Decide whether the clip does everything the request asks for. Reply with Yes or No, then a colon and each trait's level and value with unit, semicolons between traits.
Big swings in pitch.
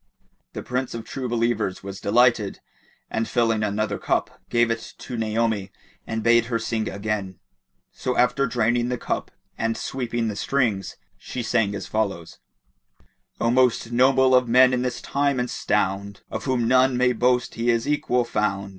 No: narrow, 2.6 semitones